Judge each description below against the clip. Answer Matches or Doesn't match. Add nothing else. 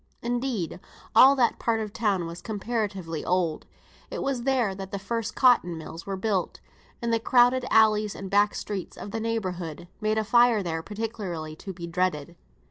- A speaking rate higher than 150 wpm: Matches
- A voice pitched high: Matches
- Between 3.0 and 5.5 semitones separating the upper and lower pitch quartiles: Matches